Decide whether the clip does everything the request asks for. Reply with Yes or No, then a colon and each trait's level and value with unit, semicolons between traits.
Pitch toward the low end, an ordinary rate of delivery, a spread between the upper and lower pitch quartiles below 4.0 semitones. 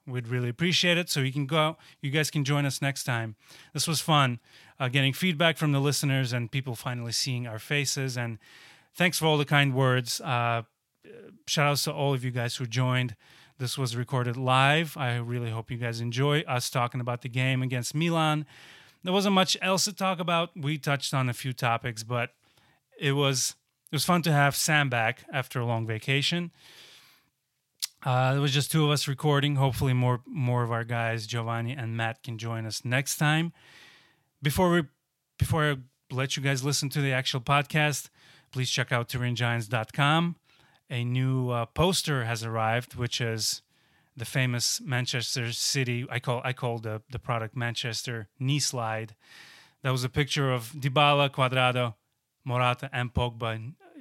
Yes: low, 130 Hz; average, 180 wpm; average, 3.2 semitones